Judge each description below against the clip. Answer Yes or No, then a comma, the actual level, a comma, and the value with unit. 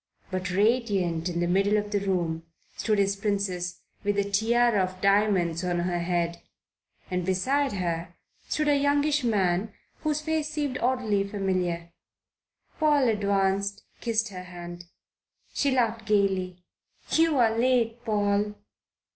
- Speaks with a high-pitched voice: Yes, high, 200 Hz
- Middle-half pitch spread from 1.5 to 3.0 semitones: No, average, 4.4 semitones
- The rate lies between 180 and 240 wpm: No, slow, 135 wpm